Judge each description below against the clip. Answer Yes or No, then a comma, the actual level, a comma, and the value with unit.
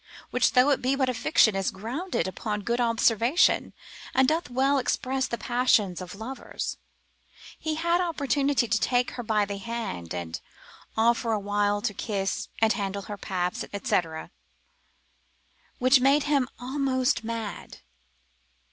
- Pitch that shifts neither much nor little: Yes, average, 4.5 semitones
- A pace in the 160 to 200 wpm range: No, average, 145 wpm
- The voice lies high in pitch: Yes, high, 235 Hz